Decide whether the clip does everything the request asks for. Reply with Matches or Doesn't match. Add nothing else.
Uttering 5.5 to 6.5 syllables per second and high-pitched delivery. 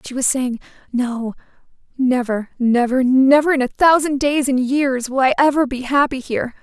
Doesn't match